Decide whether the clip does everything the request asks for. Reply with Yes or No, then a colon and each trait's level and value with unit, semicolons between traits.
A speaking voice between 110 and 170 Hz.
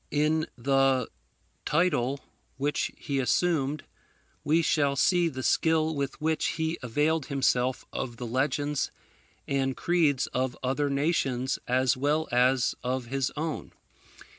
Yes: medium, 140 Hz